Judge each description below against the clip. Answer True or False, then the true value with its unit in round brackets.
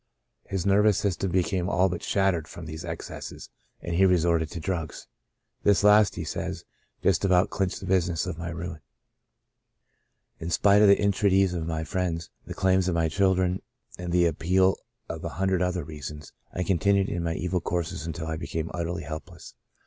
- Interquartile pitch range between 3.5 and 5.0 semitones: False (2.5 semitones)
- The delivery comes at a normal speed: True (180 wpm)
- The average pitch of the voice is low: True (90 Hz)